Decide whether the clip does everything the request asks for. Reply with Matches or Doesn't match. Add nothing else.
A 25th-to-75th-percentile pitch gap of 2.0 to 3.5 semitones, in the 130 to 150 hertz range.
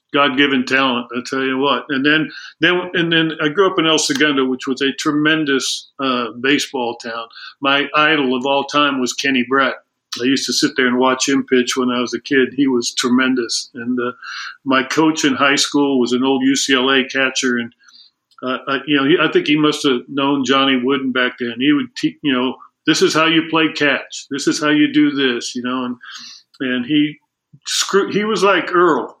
Matches